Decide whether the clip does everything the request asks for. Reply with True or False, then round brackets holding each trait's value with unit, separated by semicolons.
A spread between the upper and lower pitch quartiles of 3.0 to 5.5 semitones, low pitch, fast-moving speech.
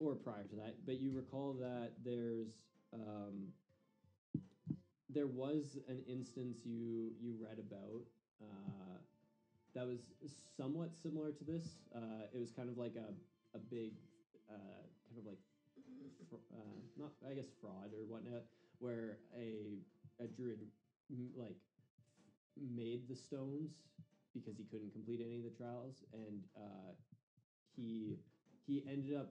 False (3.7 semitones; 120 Hz; 140 wpm)